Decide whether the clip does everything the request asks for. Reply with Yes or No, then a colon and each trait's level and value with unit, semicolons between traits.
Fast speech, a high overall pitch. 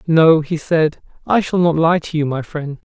No: fast, 225 wpm; medium, 160 Hz